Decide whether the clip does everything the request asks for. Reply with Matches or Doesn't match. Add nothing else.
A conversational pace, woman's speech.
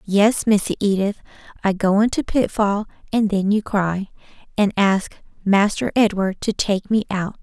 Matches